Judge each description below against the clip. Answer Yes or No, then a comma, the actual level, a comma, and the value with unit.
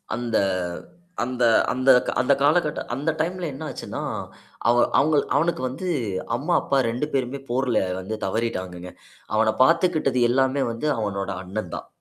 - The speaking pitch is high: No, low, 130 Hz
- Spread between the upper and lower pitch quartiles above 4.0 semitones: Yes, average, 4.9 semitones